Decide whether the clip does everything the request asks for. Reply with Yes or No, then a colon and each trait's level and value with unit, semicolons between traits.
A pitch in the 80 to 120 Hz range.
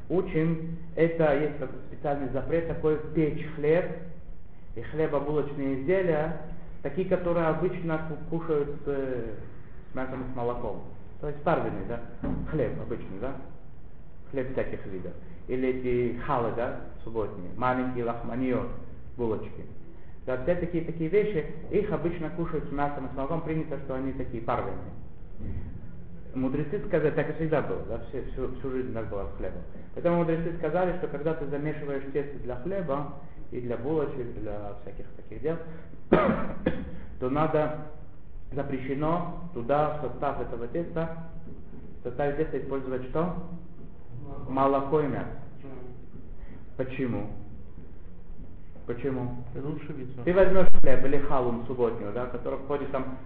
No: low, 135 Hz